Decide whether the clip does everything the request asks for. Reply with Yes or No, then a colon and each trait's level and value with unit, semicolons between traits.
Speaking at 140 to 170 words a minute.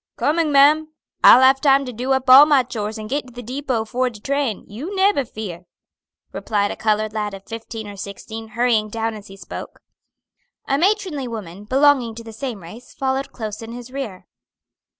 No: average, 190 wpm